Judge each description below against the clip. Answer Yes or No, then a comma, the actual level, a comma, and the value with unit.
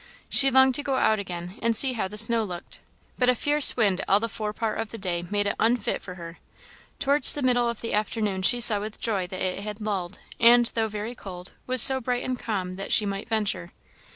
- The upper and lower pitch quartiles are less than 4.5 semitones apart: Yes, average, 3.7 semitones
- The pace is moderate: No, fast, 235 wpm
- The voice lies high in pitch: Yes, high, 215 Hz